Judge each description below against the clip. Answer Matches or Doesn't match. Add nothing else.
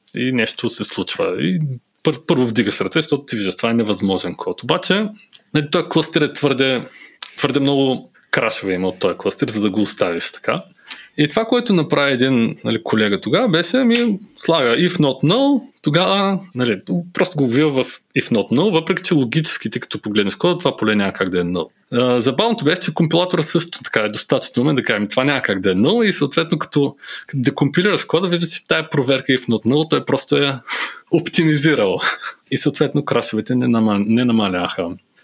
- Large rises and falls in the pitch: Matches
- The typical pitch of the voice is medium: Matches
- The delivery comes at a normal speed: Doesn't match